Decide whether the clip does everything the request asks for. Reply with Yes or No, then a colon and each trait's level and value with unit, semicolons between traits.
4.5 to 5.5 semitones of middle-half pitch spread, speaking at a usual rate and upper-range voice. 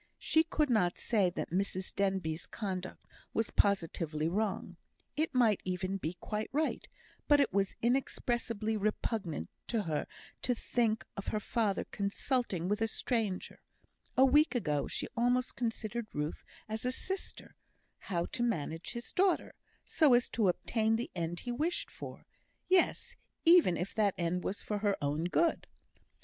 Yes: average, 5.0 semitones; average, 155 wpm; high, 215 Hz